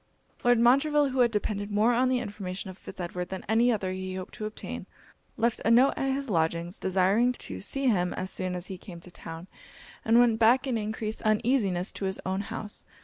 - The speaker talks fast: Yes, fast, 210 wpm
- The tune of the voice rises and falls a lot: No, average, 4.4 semitones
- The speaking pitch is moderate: No, high, 210 Hz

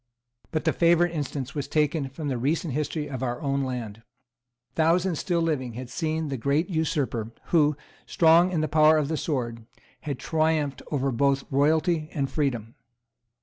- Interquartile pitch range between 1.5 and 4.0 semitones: Yes, average, 3.2 semitones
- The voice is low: No, medium, 150 Hz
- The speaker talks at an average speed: Yes, average, 165 wpm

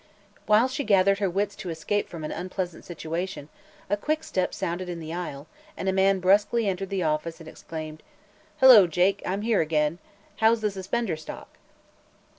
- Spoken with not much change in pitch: No, average, 3.8 semitones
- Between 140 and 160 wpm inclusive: No, average, 175 wpm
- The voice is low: No, medium, 185 Hz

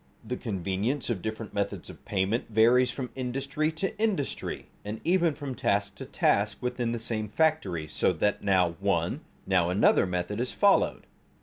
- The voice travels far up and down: No, average, 5.0 semitones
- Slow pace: No, average, 170 wpm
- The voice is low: Yes, low, 115 Hz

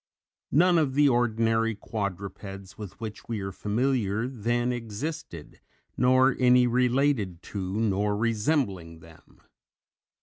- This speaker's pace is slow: Yes, slow, 110 wpm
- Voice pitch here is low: Yes, low, 115 Hz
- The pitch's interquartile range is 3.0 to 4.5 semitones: Yes, average, 4.0 semitones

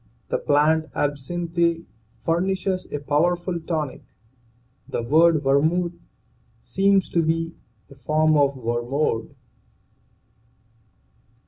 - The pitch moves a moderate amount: Yes, average, 3.1 semitones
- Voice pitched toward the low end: No, medium, 160 Hz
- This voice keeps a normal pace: No, slow, 90 wpm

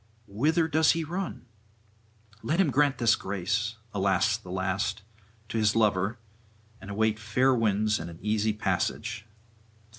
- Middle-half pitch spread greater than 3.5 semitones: Yes, average, 4.6 semitones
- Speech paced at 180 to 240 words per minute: No, average, 140 wpm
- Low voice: Yes, low, 110 Hz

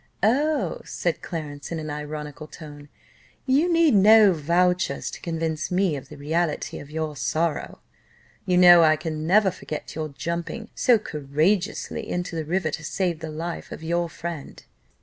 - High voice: No, medium, 165 Hz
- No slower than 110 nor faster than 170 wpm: Yes, average, 160 wpm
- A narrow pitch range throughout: No, average, 3.1 semitones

